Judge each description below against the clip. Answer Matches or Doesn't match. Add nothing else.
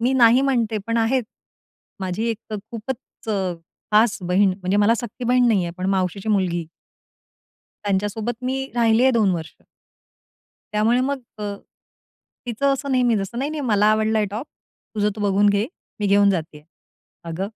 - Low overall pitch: Doesn't match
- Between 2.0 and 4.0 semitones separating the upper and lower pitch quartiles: Matches